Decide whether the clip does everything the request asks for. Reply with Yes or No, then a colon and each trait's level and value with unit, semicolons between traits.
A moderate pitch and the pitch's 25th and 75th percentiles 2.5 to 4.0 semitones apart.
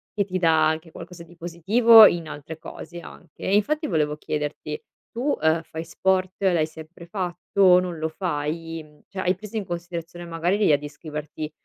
Yes: medium, 170 Hz; average, 2.9 semitones